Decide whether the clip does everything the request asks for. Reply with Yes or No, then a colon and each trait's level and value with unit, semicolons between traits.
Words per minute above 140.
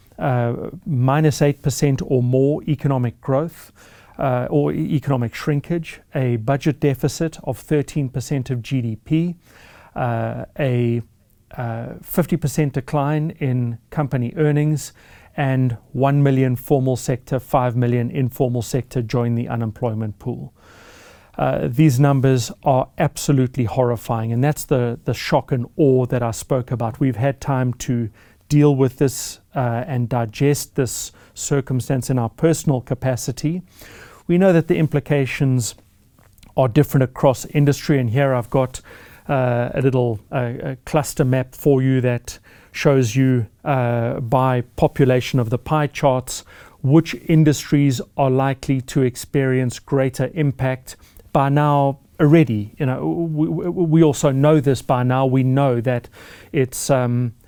No: slow, 135 wpm